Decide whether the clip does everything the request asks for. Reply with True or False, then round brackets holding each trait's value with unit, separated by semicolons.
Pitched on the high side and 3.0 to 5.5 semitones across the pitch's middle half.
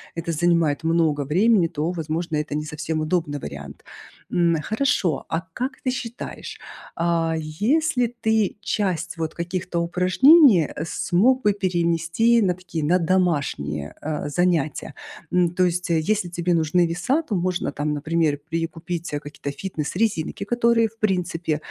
False (170 Hz; 3.4 semitones)